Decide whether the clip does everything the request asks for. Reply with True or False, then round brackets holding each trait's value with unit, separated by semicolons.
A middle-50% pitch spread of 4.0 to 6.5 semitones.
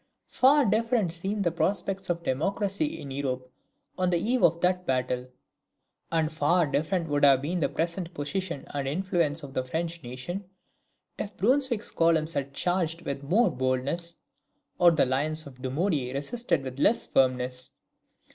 True (5.2 semitones)